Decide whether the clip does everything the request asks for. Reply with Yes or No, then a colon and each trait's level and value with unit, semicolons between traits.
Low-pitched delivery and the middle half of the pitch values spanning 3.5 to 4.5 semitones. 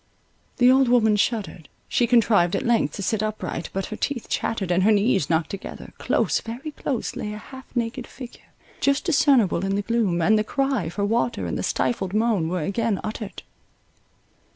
No: high, 220 Hz; average, 3.8 semitones